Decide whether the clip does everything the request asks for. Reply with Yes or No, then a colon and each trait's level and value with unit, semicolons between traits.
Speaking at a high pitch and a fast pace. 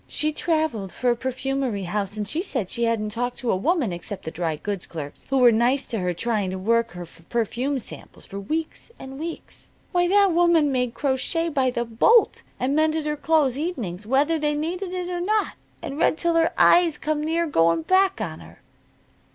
Yes: very high, 265 Hz; fast, 210 wpm